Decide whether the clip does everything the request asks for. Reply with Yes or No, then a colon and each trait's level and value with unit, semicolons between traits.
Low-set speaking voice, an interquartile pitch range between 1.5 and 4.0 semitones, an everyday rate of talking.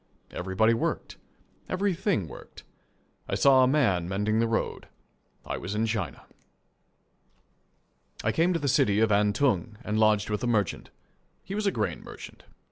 No: low, 110 Hz; average, 5.3 semitones; average, 150 wpm